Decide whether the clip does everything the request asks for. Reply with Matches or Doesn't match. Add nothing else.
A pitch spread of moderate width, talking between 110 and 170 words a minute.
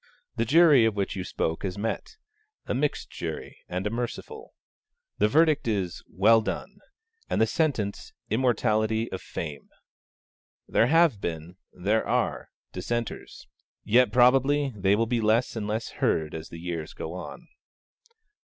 Matches